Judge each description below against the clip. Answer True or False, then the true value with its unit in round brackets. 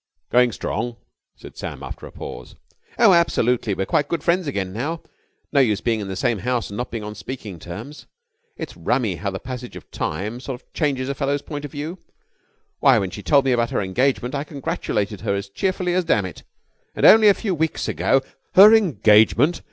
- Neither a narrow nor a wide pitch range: False (6.0 semitones)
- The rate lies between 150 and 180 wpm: False (200 wpm)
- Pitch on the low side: True (125 Hz)